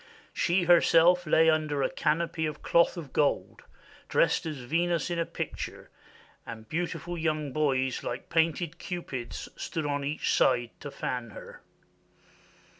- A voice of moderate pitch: Yes, medium, 155 Hz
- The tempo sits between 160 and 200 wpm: No, average, 140 wpm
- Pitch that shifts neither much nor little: Yes, average, 3.4 semitones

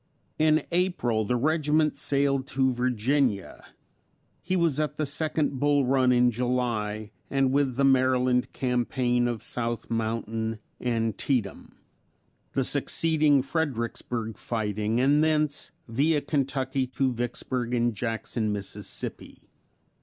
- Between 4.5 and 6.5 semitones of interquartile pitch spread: No, average, 3.4 semitones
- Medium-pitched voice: No, low, 130 Hz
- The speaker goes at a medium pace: No, slow, 115 wpm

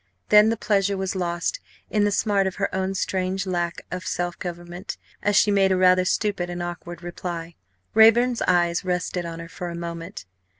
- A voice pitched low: No, medium, 185 Hz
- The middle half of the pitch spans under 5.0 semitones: Yes, narrow, 2.4 semitones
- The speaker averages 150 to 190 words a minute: Yes, average, 185 wpm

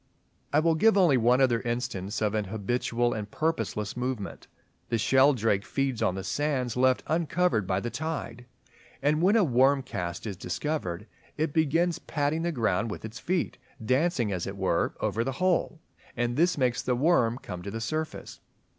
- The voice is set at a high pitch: No, low, 125 Hz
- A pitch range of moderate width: No, wide, 6.2 semitones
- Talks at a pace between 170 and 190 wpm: Yes, average, 180 wpm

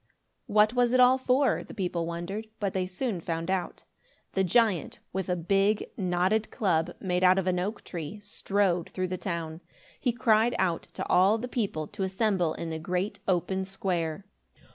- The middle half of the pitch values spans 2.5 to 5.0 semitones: Yes, average, 3.3 semitones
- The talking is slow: No, average, 180 wpm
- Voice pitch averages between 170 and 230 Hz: Yes, high, 190 Hz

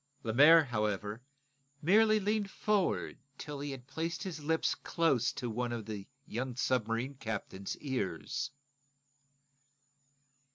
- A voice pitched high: No, low, 130 Hz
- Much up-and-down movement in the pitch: Yes, wide, 6.3 semitones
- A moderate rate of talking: No, slow, 115 wpm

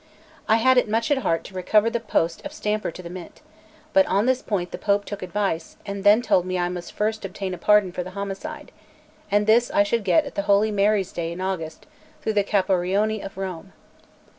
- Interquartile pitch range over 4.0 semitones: No, narrow, 2.6 semitones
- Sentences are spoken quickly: Yes, fast, 215 wpm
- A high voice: Yes, high, 200 Hz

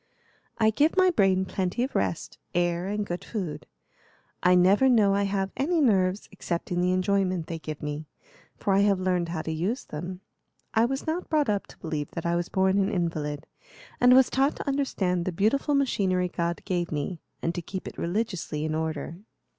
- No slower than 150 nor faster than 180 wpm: No, average, 195 wpm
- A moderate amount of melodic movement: Yes, average, 4.0 semitones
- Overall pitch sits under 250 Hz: Yes, medium, 185 Hz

